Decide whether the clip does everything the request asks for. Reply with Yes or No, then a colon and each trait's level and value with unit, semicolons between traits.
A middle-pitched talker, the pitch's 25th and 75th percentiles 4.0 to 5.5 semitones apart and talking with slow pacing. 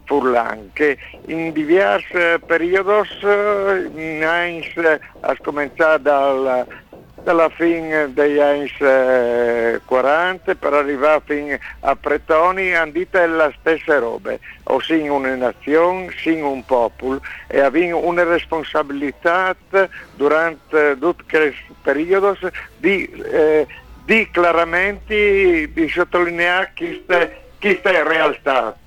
Yes: medium, 165 Hz; average, 4.4 semitones; slow, 100 wpm